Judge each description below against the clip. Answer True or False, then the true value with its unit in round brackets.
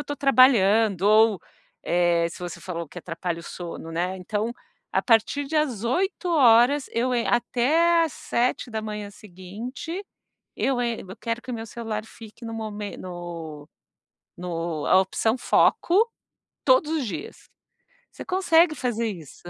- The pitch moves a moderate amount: False (6.2 semitones)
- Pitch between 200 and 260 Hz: True (225 Hz)